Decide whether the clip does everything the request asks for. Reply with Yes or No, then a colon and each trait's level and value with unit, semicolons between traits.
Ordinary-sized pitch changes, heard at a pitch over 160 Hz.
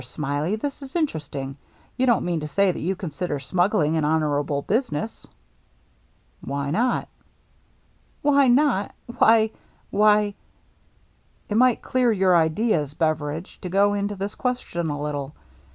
No: wide, 6.7 semitones; medium, 185 Hz